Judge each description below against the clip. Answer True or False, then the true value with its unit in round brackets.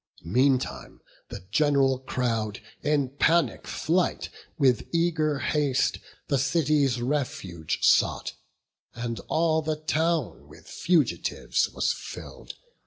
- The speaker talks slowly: True (105 wpm)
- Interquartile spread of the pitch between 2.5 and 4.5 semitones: True (3.8 semitones)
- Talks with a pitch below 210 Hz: True (140 Hz)